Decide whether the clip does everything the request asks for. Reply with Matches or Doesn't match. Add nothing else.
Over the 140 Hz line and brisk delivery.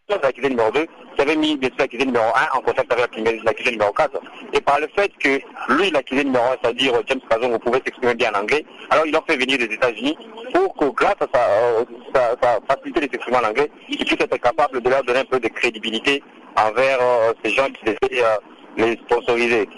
Doesn't match